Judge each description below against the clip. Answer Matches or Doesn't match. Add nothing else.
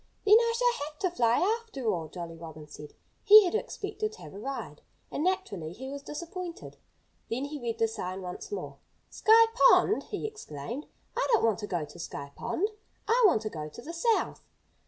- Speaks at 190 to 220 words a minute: Matches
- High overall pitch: Matches